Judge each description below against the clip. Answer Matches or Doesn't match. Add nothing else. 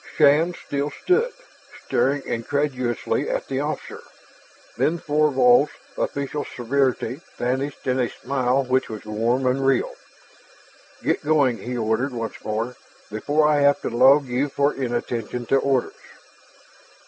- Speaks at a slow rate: Matches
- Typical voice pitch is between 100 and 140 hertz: Matches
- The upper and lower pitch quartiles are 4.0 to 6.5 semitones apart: Doesn't match